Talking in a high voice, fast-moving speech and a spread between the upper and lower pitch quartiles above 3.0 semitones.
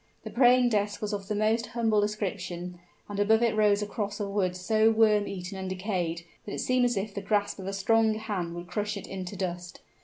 No: high, 205 Hz; fast, 225 wpm; narrow, 2.5 semitones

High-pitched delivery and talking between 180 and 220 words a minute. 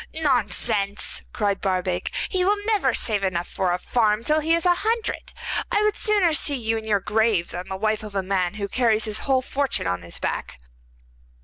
Yes: high, 220 Hz; average, 200 wpm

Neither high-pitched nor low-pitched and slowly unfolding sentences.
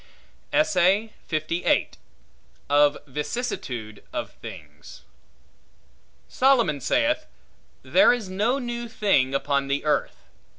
Yes: medium, 170 Hz; slow, 80 wpm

